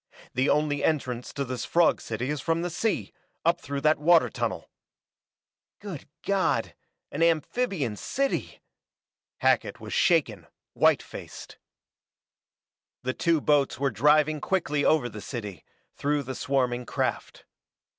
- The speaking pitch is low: No, medium, 145 Hz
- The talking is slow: Yes, slow, 130 wpm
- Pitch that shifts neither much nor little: Yes, average, 4.4 semitones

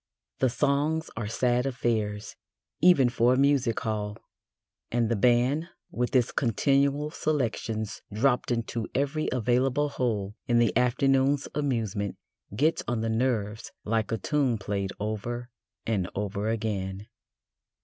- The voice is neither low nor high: No, low, 120 Hz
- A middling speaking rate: No, slow, 130 wpm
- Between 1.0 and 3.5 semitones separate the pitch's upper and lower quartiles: No, average, 3.9 semitones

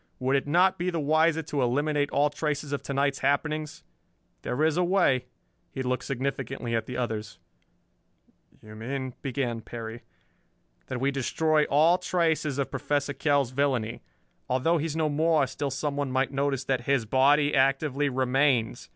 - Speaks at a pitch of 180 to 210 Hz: No, medium, 140 Hz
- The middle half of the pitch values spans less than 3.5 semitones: Yes, average, 2.8 semitones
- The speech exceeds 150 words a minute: Yes, average, 165 wpm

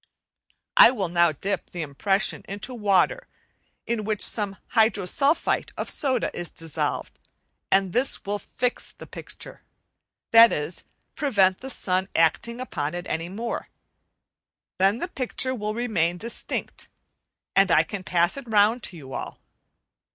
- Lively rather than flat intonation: No, average, 5.0 semitones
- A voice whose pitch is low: No, high, 200 Hz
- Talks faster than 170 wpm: No, average, 140 wpm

